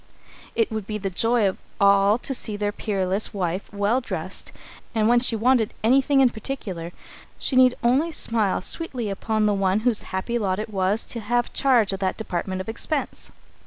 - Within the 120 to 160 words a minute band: No, average, 195 wpm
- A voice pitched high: Yes, high, 215 Hz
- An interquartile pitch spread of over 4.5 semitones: No, average, 3.7 semitones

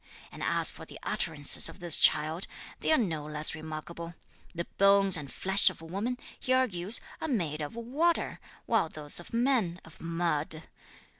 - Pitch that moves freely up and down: Yes, wide, 6.0 semitones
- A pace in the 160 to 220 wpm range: Yes, average, 165 wpm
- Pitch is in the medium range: Yes, medium, 170 Hz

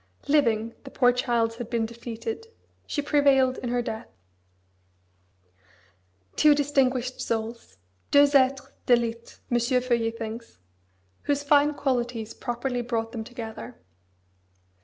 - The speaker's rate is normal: No, slow, 115 wpm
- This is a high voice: Yes, high, 245 Hz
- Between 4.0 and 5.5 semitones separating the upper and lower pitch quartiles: No, average, 2.8 semitones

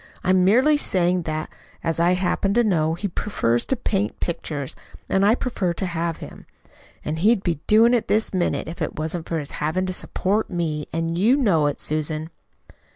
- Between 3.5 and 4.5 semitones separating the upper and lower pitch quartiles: Yes, average, 4.2 semitones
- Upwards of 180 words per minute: Yes, average, 190 wpm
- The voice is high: No, medium, 175 Hz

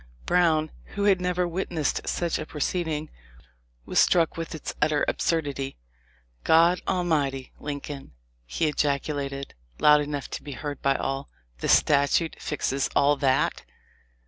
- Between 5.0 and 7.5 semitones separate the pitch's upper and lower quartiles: No, average, 2.9 semitones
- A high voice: No, medium, 150 Hz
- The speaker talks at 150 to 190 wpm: No, average, 140 wpm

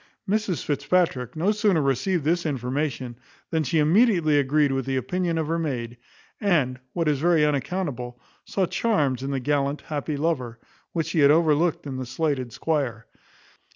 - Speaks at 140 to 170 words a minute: Yes, average, 160 wpm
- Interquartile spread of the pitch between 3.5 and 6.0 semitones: Yes, average, 4.1 semitones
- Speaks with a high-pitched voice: No, medium, 150 Hz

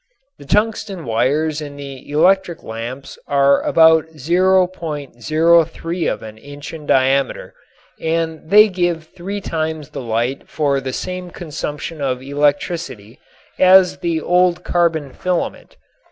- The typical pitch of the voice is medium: Yes, medium, 160 Hz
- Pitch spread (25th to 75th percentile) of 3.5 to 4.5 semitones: Yes, average, 3.9 semitones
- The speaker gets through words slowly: Yes, slow, 125 wpm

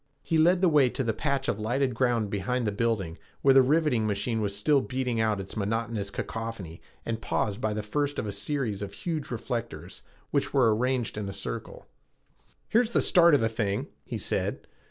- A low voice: Yes, low, 115 Hz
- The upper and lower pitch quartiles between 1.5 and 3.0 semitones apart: No, average, 4.5 semitones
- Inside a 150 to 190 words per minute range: No, average, 200 wpm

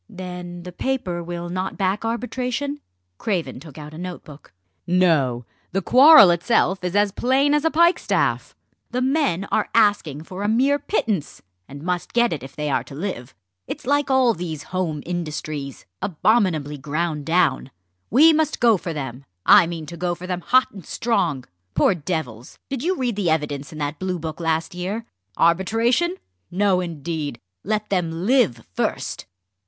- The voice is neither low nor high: Yes, medium, 180 Hz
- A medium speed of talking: Yes, average, 165 wpm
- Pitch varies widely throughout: Yes, wide, 6.5 semitones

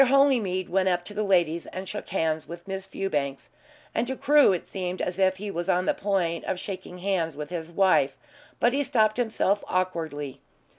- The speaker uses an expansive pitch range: No, average, 3.1 semitones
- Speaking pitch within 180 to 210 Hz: Yes, medium, 185 Hz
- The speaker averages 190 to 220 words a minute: Yes, average, 195 wpm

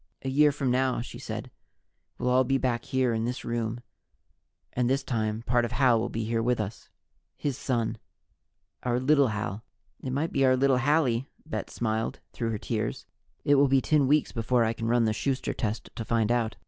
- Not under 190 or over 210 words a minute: Yes, average, 200 wpm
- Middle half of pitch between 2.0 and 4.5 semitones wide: Yes, average, 2.7 semitones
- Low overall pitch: Yes, low, 125 Hz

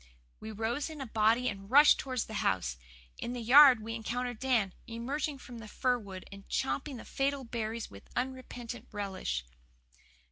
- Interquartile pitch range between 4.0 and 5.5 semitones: No, average, 3.3 semitones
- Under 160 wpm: No, average, 170 wpm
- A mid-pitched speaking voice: No, high, 235 Hz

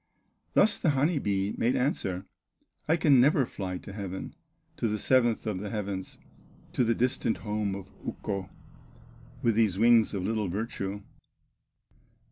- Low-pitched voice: Yes, low, 105 Hz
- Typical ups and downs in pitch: Yes, average, 3.9 semitones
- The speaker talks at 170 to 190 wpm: No, average, 145 wpm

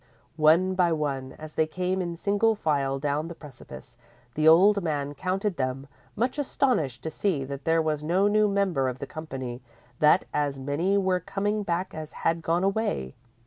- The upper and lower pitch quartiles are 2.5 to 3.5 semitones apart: No, average, 5.0 semitones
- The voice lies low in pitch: No, medium, 160 Hz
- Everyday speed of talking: Yes, average, 185 wpm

